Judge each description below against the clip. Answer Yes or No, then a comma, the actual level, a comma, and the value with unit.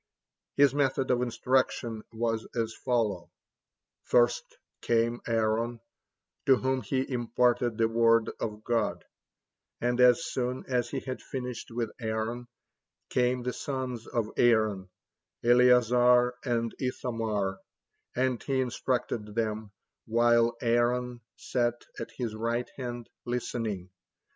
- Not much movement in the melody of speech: Yes, narrow, 1.7 semitones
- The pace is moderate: No, slow, 115 wpm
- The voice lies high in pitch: No, low, 120 Hz